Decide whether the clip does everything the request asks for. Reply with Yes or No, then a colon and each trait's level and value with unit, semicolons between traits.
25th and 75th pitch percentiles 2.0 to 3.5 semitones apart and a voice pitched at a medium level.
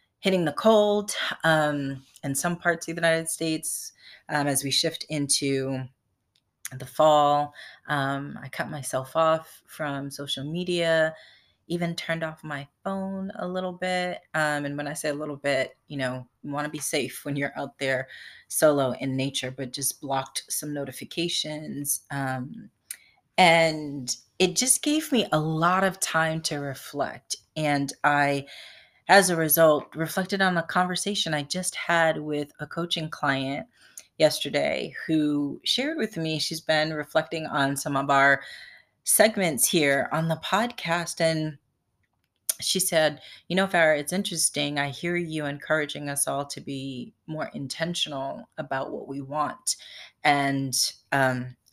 Yes: average, 3.1 semitones; medium, 150 Hz